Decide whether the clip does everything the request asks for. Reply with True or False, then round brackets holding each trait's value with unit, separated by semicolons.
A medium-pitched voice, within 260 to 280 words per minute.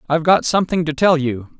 False (155 Hz; 225 wpm)